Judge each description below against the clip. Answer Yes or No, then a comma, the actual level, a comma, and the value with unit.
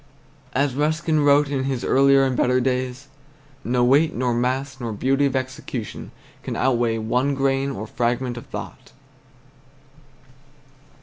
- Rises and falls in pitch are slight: Yes, narrow, 2.1 semitones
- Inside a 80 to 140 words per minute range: Yes, slow, 135 wpm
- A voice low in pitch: Yes, low, 130 Hz